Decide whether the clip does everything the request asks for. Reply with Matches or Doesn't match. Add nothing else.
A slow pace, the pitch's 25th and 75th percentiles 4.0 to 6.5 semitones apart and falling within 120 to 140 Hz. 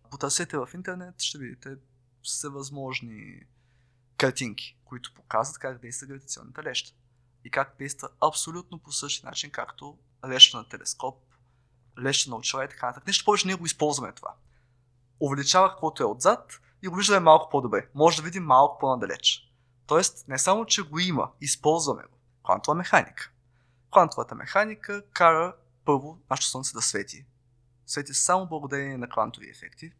Doesn't match